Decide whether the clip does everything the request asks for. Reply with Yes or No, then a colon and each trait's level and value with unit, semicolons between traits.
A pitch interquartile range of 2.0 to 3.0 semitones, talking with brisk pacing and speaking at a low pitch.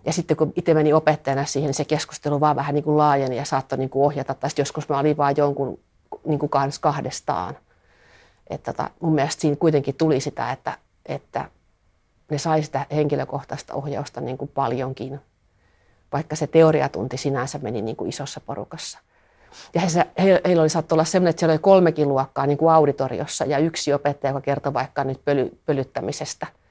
No: narrow, 2.4 semitones; fast, 170 wpm; medium, 145 Hz